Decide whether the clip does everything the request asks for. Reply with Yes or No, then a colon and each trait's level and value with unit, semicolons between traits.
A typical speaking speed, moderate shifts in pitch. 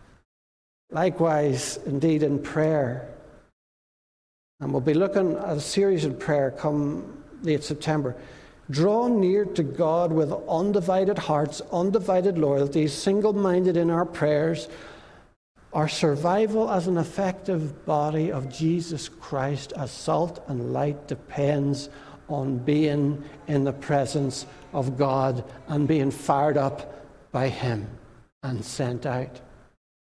No: slow, 115 wpm; average, 3.4 semitones